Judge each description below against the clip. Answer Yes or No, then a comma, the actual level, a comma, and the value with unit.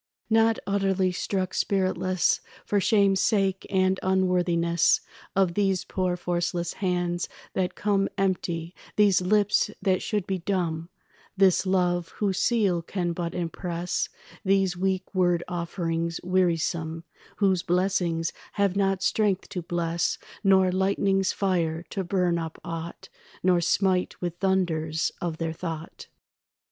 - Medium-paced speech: No, slow, 125 wpm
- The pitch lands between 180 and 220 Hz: Yes, medium, 185 Hz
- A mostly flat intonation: Yes, narrow, 2.0 semitones